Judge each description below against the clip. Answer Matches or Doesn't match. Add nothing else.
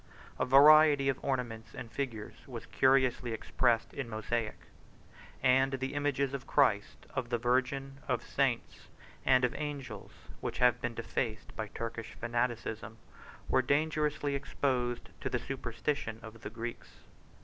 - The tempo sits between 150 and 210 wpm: Doesn't match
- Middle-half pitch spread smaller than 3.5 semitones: Matches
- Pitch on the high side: Doesn't match